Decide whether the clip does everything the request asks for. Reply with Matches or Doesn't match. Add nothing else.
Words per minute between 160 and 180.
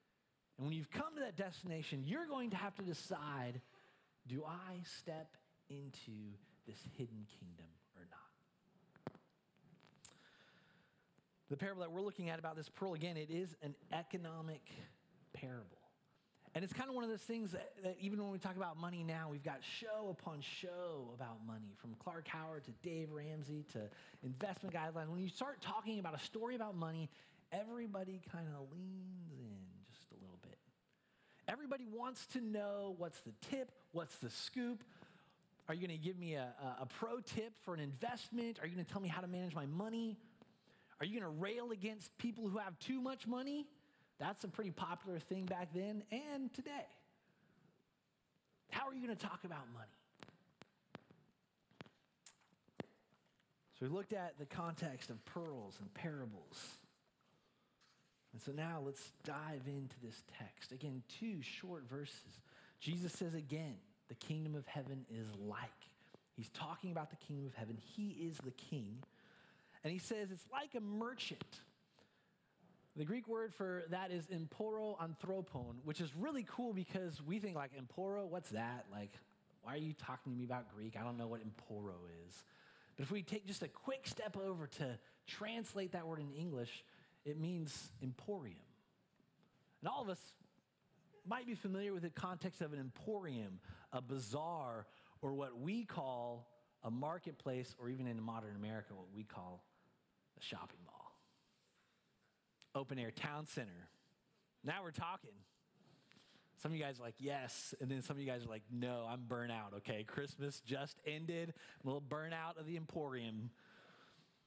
Matches